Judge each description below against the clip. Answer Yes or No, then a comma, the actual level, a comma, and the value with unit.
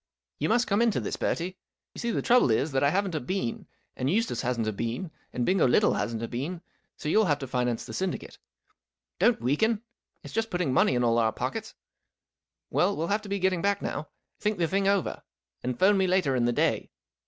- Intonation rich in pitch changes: Yes, wide, 8.0 semitones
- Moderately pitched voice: Yes, medium, 170 Hz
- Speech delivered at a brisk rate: Yes, fast, 220 wpm